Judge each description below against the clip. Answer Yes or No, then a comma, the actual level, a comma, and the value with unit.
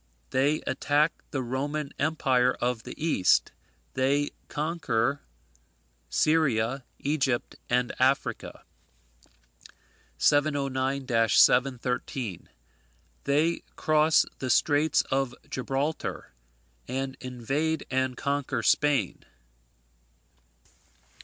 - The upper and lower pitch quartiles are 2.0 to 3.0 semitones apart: Yes, narrow, 2.6 semitones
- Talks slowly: Yes, slow, 75 wpm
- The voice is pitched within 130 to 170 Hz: Yes, low, 135 Hz